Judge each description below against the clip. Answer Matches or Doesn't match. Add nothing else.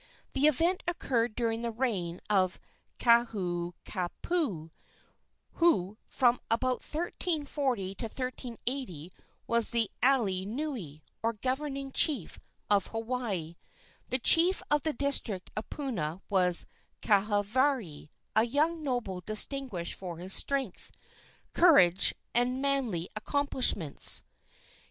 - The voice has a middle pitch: Doesn't match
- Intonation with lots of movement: Matches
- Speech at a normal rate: Doesn't match